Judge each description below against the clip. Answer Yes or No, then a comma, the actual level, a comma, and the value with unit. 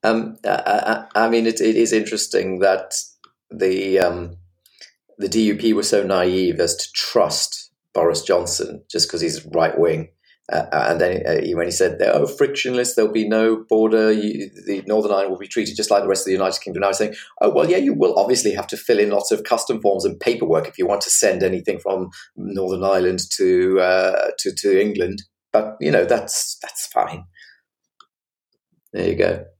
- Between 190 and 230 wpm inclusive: Yes, average, 200 wpm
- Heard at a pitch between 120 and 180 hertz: No, low, 110 Hz